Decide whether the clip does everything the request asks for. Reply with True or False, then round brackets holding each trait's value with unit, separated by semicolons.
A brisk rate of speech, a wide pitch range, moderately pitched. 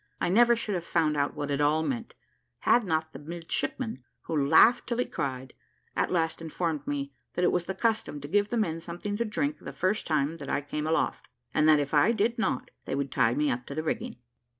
True (230 wpm; 5.8 semitones; 160 Hz)